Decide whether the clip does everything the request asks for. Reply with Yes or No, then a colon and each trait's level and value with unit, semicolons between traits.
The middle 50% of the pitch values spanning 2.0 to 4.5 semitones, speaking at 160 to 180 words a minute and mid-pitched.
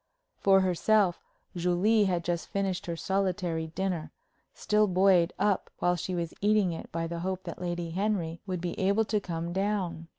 Yes: narrow, 2.5 semitones; average, 170 wpm; medium, 180 Hz